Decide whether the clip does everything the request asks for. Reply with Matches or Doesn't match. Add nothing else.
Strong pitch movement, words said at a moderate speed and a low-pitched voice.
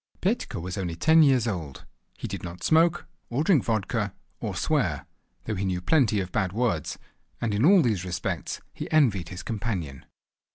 Matches